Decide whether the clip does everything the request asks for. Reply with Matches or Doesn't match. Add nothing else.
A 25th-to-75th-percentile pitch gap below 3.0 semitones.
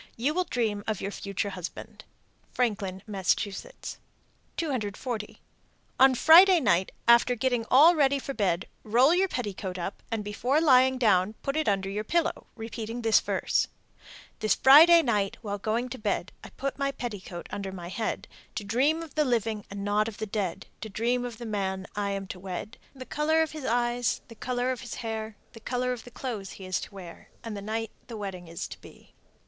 Doesn't match